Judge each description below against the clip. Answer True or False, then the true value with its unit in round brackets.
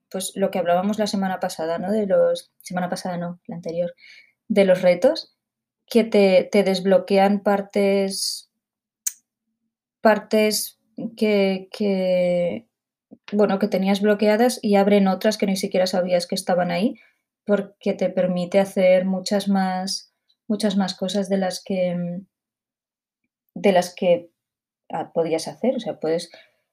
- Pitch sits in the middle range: False (195 Hz)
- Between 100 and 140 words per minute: True (135 wpm)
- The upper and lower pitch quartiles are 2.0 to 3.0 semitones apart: True (2.7 semitones)